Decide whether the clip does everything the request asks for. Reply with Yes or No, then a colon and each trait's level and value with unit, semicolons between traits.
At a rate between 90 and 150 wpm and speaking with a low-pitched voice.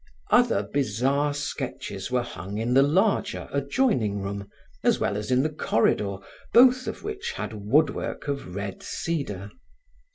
Yes: average, 140 wpm; low, 130 Hz